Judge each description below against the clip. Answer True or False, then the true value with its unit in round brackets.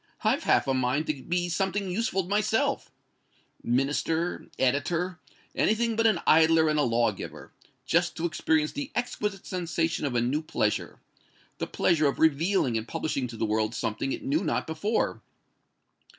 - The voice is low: False (160 Hz)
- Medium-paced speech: True (160 wpm)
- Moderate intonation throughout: False (5.7 semitones)